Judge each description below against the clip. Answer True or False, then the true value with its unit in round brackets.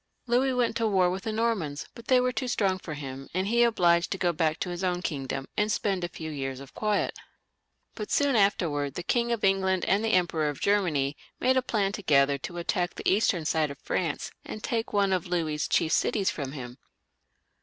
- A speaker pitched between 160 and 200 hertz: True (185 Hz)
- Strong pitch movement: True (5.7 semitones)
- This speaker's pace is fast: True (220 wpm)